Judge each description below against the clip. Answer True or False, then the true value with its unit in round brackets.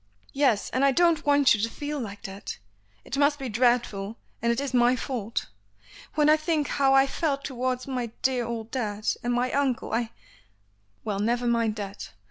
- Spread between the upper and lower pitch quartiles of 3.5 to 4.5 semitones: True (3.8 semitones)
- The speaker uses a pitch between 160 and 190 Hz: False (245 Hz)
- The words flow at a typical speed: True (190 wpm)